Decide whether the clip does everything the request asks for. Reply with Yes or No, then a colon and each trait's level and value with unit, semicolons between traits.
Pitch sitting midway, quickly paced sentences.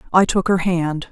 Yes: medium, 175 Hz; fast, 215 wpm